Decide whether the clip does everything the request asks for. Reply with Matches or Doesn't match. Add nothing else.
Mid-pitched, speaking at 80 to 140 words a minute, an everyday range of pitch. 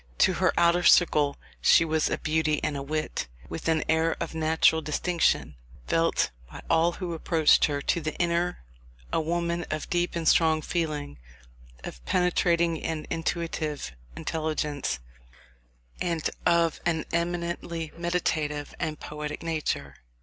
Doesn't match